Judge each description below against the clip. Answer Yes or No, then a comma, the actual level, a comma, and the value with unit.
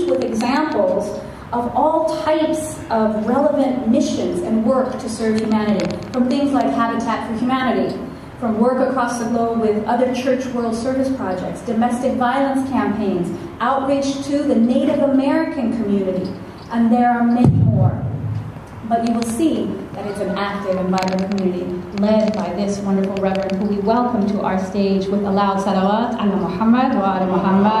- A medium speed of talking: Yes, average, 160 wpm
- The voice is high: Yes, high, 230 Hz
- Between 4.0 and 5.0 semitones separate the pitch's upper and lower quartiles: Yes, average, 4.7 semitones